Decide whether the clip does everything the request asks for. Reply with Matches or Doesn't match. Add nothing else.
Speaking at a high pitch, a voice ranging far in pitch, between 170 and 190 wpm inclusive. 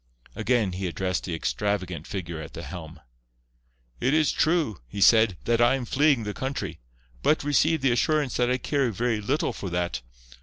Doesn't match